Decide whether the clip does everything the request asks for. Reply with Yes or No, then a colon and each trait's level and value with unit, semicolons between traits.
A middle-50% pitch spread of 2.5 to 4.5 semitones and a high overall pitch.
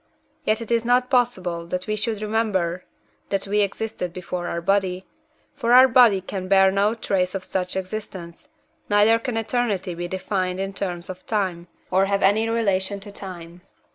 Yes: average, 3.2 semitones; high, 195 Hz